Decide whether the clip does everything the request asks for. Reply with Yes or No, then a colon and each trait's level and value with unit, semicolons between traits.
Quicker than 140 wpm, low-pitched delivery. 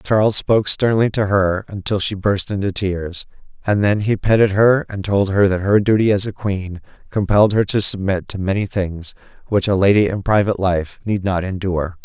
Yes: average, 200 wpm; low, 100 Hz